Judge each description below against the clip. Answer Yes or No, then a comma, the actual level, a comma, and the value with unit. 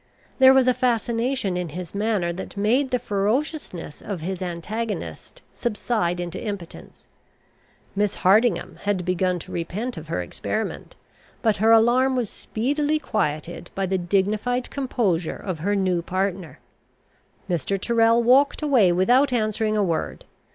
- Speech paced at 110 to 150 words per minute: Yes, average, 140 wpm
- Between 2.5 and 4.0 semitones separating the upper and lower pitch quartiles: No, average, 5.1 semitones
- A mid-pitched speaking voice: No, high, 205 Hz